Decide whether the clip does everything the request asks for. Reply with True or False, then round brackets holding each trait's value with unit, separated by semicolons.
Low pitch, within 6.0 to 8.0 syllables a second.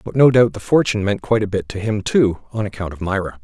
True (105 Hz; 6.5 syllables/s)